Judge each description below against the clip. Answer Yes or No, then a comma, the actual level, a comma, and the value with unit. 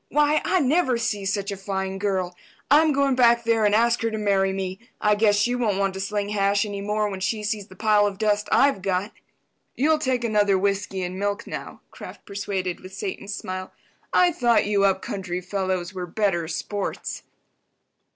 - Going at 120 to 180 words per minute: No, average, 190 wpm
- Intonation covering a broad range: No, average, 2.8 semitones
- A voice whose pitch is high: Yes, high, 205 Hz